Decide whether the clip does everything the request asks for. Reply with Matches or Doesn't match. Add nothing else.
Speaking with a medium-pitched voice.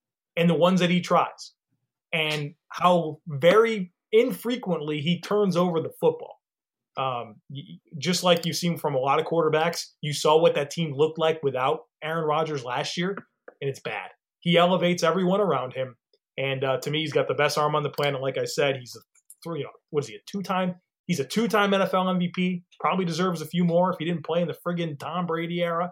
Matches